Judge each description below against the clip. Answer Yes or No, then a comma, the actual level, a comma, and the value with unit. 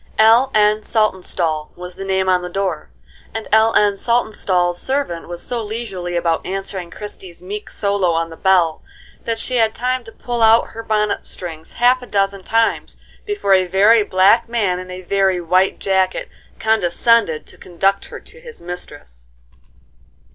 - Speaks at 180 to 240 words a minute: No, average, 165 wpm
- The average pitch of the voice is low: No, high, 195 Hz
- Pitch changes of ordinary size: Yes, average, 3.8 semitones